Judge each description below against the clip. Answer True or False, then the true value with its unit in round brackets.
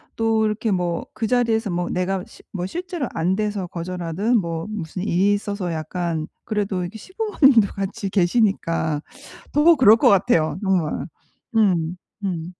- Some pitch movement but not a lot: True (4.2 semitones)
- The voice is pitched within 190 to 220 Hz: True (195 Hz)